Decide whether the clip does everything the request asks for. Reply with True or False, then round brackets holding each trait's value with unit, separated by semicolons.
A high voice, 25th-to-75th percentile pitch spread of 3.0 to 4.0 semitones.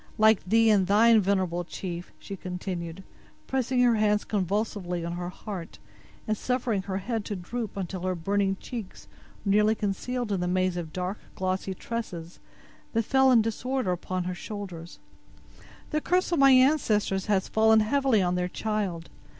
True (200 Hz; 3.7 semitones)